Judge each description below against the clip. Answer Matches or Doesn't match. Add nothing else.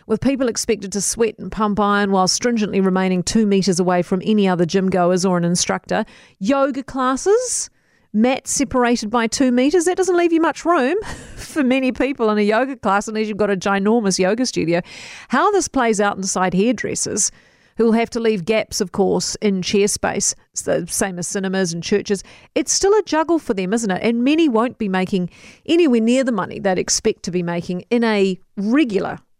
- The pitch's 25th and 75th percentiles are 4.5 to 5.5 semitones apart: Matches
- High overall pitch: Matches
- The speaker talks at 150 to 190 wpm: Doesn't match